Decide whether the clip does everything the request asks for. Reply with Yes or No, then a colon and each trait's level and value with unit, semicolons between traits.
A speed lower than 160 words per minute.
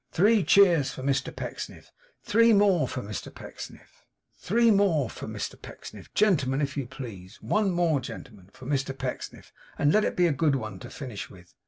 No: average, 180 wpm